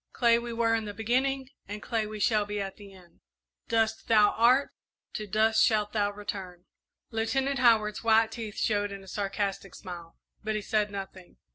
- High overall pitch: Yes, high, 215 Hz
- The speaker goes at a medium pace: Yes, average, 180 wpm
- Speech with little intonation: Yes, narrow, 2.0 semitones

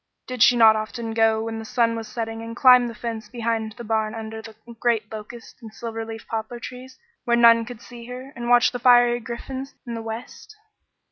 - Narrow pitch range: Yes, narrow, 1.5 semitones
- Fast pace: Yes, fast, 210 wpm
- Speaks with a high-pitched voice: Yes, high, 230 Hz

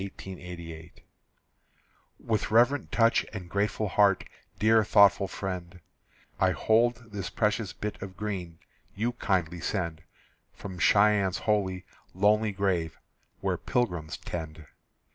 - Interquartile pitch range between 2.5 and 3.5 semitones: Yes, average, 3.2 semitones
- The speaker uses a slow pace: Yes, slow, 110 wpm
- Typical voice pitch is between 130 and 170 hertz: No, low, 100 Hz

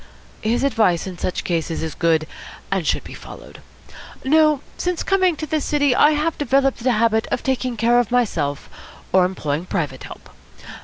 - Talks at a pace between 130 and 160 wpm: No, average, 170 wpm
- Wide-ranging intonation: Yes, wide, 8.5 semitones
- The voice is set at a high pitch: Yes, high, 235 Hz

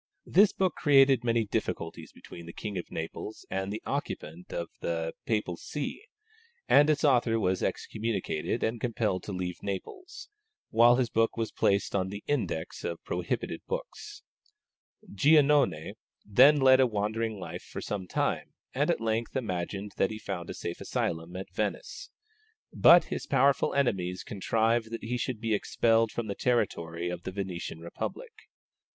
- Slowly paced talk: No, average, 160 wpm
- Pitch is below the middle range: Yes, low, 110 Hz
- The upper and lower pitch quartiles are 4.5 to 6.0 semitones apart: Yes, average, 5.1 semitones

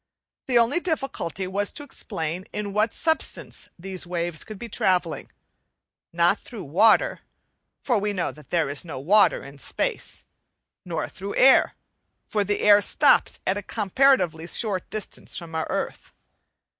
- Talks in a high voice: Yes, high, 195 Hz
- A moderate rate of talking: Yes, average, 150 wpm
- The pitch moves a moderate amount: Yes, average, 4.2 semitones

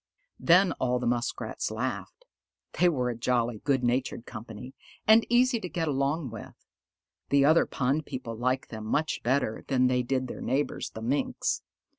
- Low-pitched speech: Yes, low, 130 Hz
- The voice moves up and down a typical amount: Yes, average, 3.9 semitones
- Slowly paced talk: No, average, 165 wpm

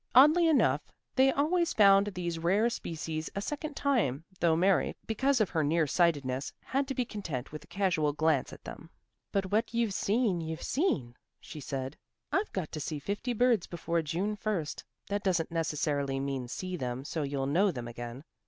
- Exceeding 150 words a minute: Yes, average, 180 wpm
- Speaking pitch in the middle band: Yes, medium, 170 Hz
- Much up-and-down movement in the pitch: Yes, wide, 6.6 semitones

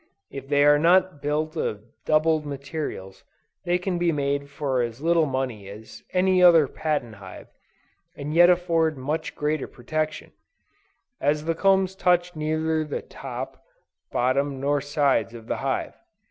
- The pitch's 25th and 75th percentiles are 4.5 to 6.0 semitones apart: No, average, 3.5 semitones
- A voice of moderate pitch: Yes, medium, 150 Hz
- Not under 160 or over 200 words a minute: No, average, 145 wpm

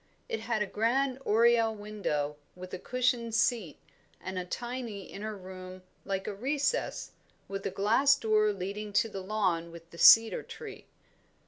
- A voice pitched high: Yes, high, 210 Hz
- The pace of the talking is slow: No, average, 155 wpm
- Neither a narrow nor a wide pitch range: Yes, average, 3.9 semitones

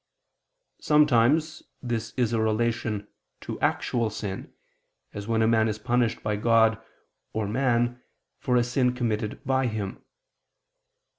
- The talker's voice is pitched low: Yes, low, 115 Hz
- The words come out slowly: Yes, slow, 130 wpm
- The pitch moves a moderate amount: No, narrow, 2.1 semitones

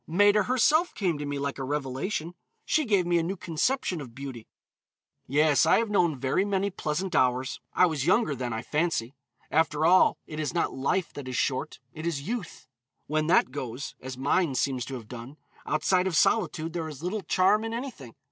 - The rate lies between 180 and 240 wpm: Yes, average, 195 wpm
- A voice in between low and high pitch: Yes, medium, 155 Hz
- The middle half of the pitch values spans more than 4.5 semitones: Yes, wide, 5.6 semitones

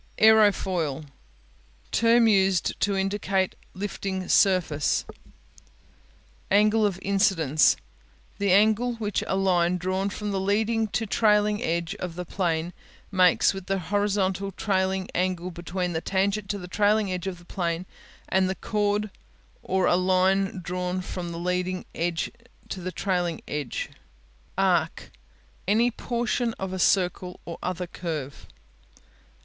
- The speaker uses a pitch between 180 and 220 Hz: Yes, high, 190 Hz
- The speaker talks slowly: Yes, slow, 130 wpm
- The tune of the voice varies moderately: No, narrow, 2.3 semitones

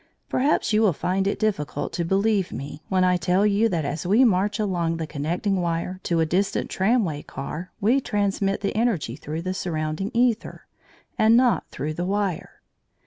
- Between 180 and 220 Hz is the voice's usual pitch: Yes, medium, 185 Hz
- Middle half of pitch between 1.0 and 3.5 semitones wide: No, average, 4.1 semitones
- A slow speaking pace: No, average, 180 wpm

